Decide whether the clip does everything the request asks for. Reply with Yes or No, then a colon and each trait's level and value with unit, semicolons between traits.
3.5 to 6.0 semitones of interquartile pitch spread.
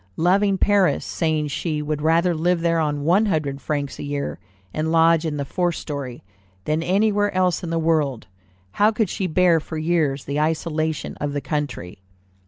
No: average, 3.0 semitones